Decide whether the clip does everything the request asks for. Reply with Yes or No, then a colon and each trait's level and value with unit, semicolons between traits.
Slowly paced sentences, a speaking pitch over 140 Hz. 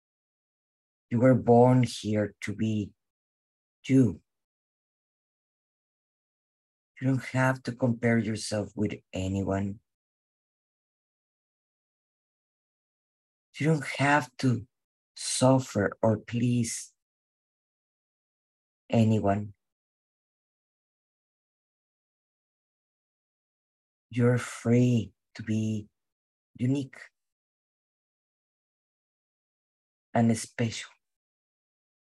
No: slow, 55 wpm; low, 110 Hz